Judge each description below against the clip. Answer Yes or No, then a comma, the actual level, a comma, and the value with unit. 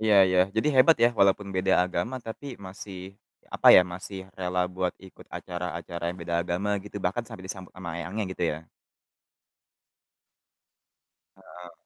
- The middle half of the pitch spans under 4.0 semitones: Yes, narrow, 2.4 semitones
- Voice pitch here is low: Yes, very low, 95 Hz